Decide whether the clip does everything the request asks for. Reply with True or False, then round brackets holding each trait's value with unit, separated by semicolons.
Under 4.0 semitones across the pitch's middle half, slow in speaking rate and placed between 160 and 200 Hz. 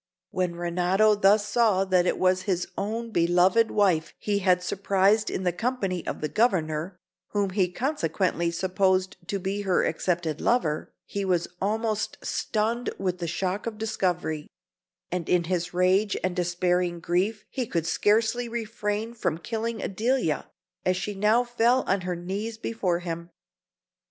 False (3.4 semitones; 155 wpm; 190 Hz)